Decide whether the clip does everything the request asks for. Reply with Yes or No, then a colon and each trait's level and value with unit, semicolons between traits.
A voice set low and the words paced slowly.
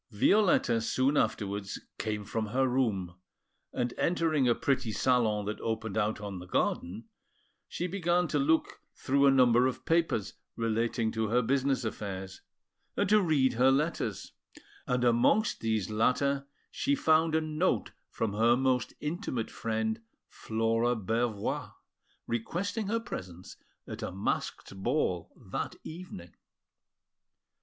Yes: low, 120 Hz; slow, 130 wpm